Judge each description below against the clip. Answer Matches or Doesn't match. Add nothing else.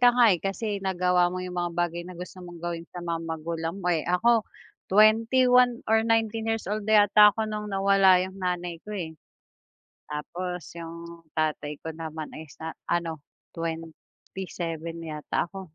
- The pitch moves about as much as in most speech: Matches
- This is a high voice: Doesn't match